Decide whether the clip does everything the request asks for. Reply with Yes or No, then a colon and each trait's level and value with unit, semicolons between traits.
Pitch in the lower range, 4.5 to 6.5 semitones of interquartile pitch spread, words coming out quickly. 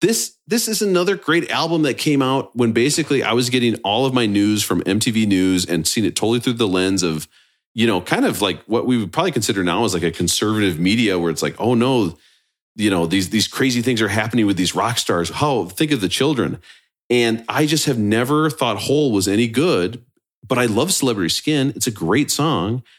Yes: low, 115 Hz; average, 5.1 semitones; fast, 225 wpm